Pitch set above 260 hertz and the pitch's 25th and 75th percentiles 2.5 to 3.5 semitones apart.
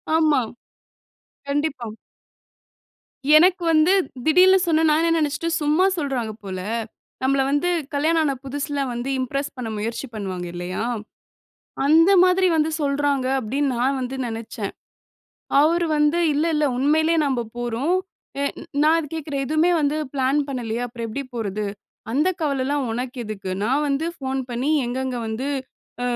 No: very high, 280 Hz; average, 4.2 semitones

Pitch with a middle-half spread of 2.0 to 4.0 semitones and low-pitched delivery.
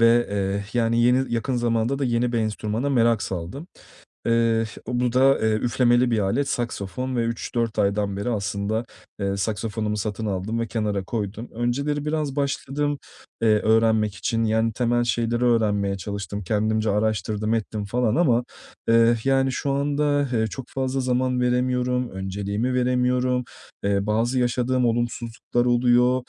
Yes: average, 2.8 semitones; low, 115 Hz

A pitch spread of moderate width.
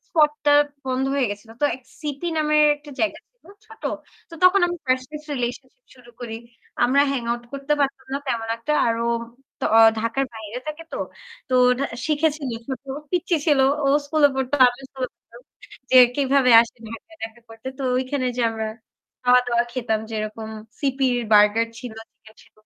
Yes: average, 3.9 semitones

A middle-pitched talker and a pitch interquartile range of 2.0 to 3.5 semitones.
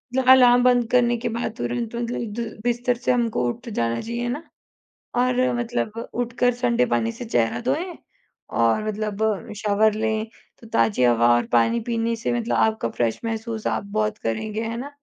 No: high, 230 Hz; narrow, 2.4 semitones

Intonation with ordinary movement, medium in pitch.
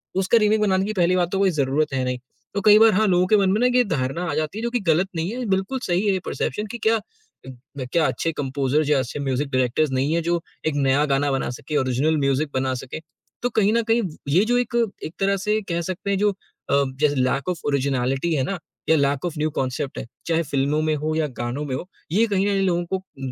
No: wide, 6.0 semitones; medium, 160 Hz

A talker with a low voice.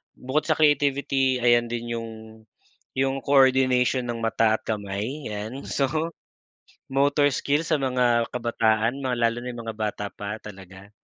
Yes: low, 120 Hz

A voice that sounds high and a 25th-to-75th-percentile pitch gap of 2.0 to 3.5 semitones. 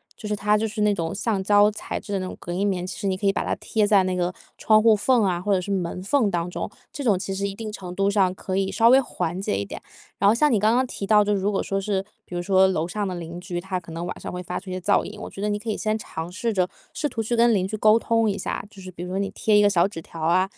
Yes: high, 195 Hz; narrow, 2.6 semitones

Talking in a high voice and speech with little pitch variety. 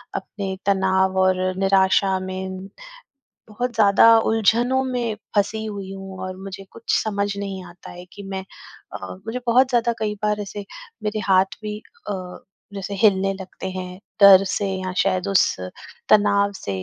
Yes: high, 195 Hz; narrow, 1.9 semitones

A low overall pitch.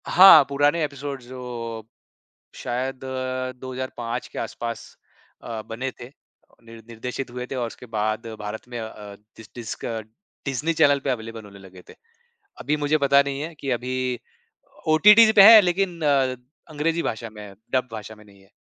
Yes: low, 125 Hz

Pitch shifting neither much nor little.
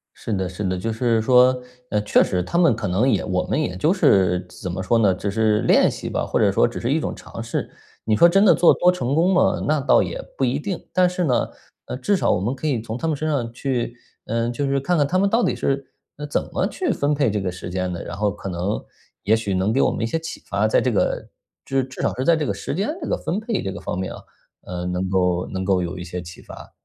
No: wide, 7.6 semitones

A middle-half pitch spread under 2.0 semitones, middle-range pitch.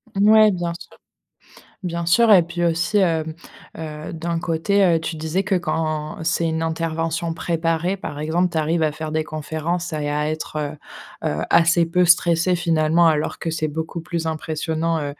Yes: narrow, 1.6 semitones; medium, 165 Hz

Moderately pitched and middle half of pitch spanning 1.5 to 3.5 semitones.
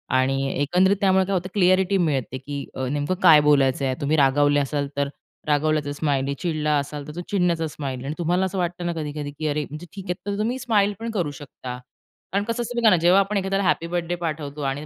No: medium, 155 Hz; average, 4.6 semitones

